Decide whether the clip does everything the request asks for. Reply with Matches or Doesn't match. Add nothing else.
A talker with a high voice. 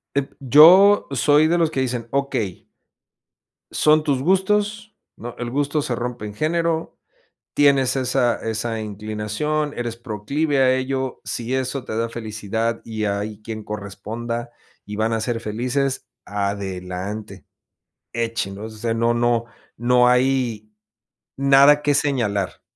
Doesn't match